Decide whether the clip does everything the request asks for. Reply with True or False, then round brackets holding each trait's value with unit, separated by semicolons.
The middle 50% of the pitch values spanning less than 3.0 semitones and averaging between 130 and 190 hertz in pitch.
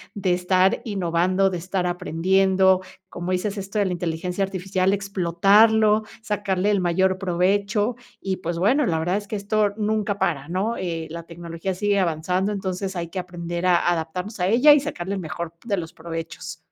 True (2.6 semitones; 185 Hz)